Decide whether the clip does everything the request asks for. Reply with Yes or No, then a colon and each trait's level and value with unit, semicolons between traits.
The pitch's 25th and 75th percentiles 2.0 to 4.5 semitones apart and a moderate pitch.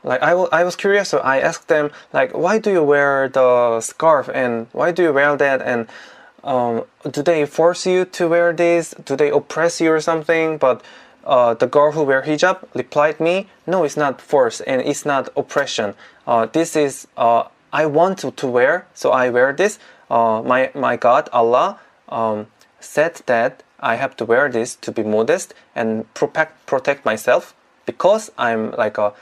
No: wide, 5.5 semitones; medium, 145 Hz